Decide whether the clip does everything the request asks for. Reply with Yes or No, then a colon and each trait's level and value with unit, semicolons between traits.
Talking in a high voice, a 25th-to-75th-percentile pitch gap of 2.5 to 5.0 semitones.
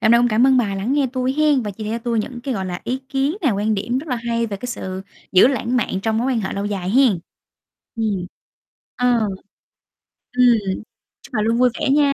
Yes: high, 235 Hz; average, 3.5 semitones